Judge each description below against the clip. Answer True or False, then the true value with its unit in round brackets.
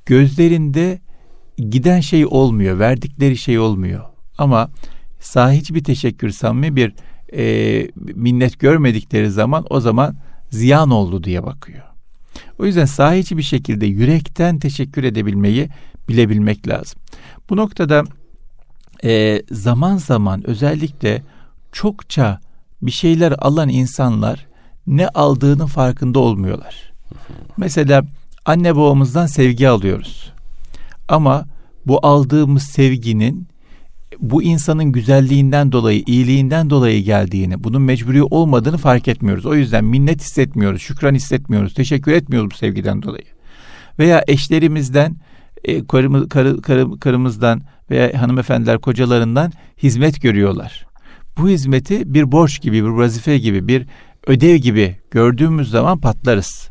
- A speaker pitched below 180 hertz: True (135 Hz)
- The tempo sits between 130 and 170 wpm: False (110 wpm)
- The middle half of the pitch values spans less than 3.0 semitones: False (4.5 semitones)